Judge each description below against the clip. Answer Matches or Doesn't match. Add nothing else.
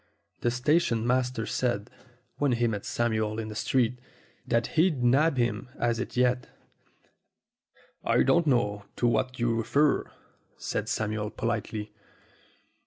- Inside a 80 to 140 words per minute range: Matches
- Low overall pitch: Matches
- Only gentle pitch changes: Matches